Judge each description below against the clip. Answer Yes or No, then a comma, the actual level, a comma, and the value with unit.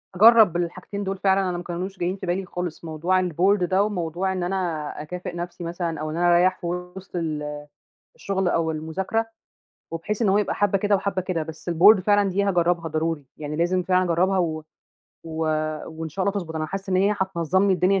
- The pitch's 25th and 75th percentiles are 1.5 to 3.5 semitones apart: Yes, narrow, 2.5 semitones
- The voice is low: No, medium, 180 Hz